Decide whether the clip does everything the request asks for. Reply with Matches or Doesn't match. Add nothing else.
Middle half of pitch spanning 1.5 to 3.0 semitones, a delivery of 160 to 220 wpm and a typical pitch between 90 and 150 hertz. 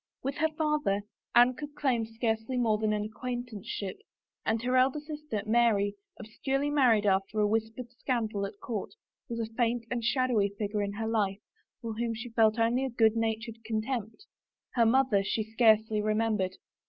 Doesn't match